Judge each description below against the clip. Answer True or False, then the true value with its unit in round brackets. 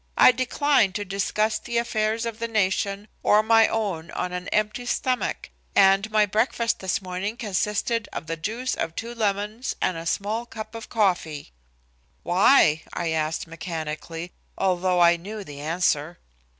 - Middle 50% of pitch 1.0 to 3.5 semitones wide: False (4.3 semitones)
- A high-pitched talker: True (200 Hz)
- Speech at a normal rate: True (155 wpm)